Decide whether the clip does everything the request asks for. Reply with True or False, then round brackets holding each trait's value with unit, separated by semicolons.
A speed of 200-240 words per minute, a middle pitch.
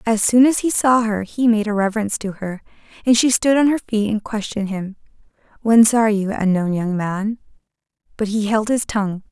False (205 wpm; 215 Hz)